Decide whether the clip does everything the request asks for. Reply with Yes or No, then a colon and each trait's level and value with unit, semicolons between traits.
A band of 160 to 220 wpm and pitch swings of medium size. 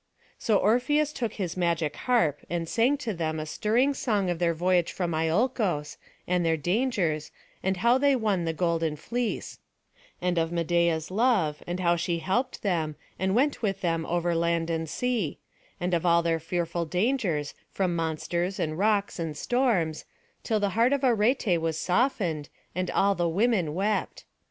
Yes: average, 170 wpm; average, 5.0 semitones